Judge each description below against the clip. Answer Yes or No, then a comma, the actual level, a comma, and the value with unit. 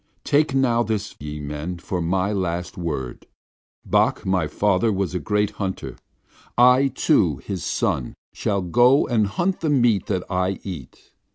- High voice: No, very low, 95 Hz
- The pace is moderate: Yes, average, 155 wpm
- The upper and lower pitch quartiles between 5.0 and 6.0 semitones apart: Yes, wide, 5.4 semitones